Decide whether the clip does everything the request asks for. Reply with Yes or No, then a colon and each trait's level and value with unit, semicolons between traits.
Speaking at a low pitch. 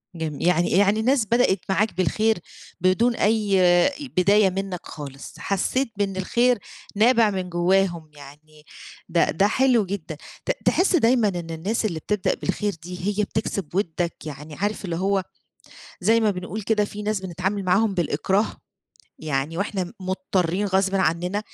No: high, 190 Hz